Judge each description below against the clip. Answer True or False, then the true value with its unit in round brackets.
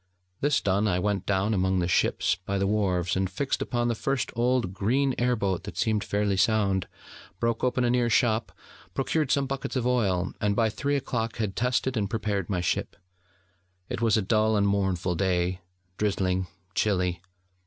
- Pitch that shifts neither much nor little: True (4.0 semitones)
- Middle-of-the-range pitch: False (105 Hz)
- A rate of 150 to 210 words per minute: True (180 wpm)